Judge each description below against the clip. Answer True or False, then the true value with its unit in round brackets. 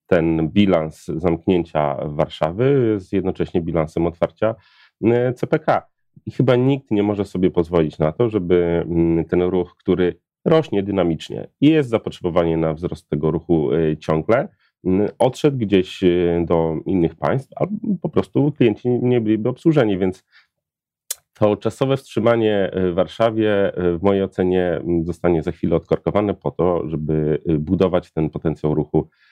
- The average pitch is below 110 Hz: True (90 Hz)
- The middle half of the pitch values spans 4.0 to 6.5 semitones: True (4.9 semitones)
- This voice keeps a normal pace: True (130 wpm)